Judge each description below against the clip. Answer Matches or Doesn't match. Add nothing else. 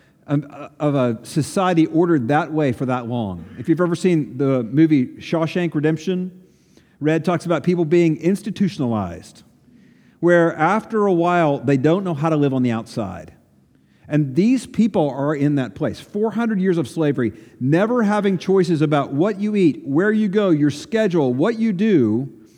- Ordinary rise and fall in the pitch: Matches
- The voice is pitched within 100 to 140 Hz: Doesn't match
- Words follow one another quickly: Doesn't match